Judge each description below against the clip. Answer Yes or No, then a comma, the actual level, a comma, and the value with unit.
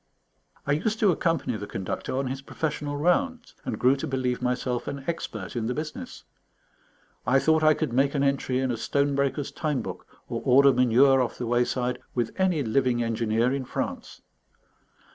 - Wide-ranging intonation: No, average, 2.9 semitones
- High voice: No, low, 135 Hz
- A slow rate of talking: No, average, 180 wpm